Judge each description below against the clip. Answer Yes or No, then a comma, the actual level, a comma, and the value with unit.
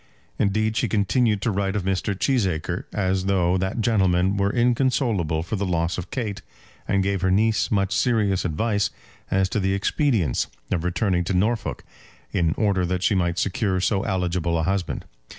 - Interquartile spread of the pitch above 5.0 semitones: No, average, 3.0 semitones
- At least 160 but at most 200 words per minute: Yes, average, 170 wpm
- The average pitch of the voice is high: No, very low, 95 Hz